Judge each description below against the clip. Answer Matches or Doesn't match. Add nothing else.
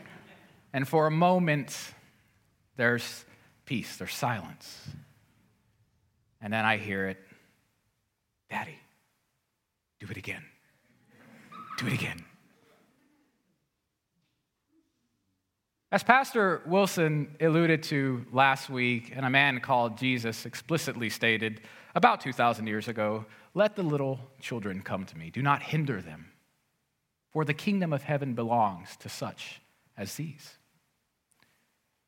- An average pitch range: Doesn't match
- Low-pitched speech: Matches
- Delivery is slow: Matches